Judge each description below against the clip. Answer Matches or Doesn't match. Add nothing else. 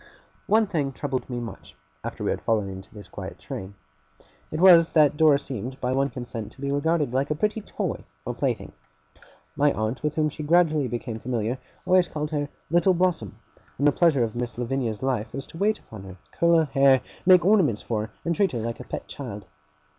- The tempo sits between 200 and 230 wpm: Matches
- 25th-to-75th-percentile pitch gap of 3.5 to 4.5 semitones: Doesn't match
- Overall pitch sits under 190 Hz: Matches